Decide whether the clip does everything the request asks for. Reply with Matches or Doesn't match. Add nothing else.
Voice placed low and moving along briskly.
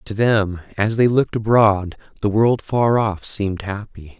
Doesn't match